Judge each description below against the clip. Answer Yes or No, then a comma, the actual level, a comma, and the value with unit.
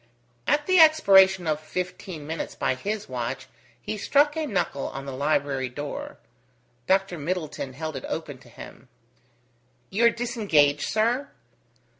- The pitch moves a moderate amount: No, wide, 7.3 semitones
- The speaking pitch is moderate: Yes, medium, 165 Hz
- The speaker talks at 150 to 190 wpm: No, average, 140 wpm